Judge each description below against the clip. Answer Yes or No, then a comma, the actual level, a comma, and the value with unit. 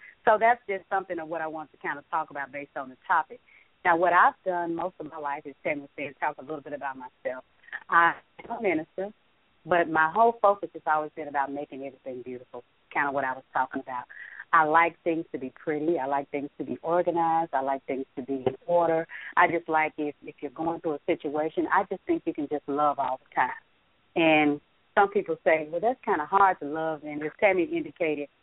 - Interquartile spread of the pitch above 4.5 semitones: No, average, 3.4 semitones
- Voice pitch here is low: No, medium, 160 Hz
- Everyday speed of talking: No, fast, 230 wpm